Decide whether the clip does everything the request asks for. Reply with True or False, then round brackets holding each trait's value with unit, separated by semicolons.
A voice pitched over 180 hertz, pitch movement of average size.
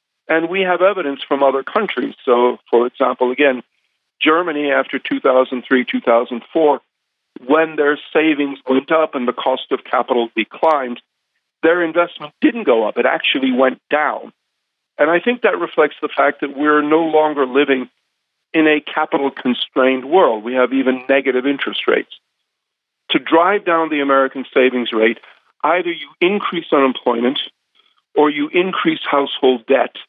False (140 Hz; 3.7 semitones)